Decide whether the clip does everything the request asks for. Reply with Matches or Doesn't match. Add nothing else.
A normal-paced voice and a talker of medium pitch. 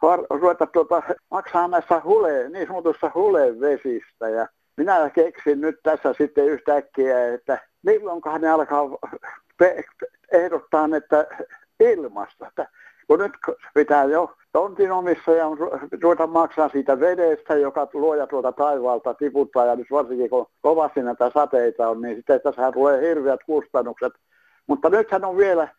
Matches